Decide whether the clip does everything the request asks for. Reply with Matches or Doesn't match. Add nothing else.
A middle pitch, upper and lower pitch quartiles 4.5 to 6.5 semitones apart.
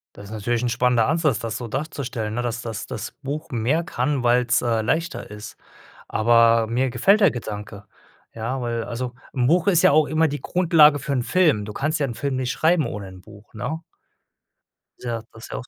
Doesn't match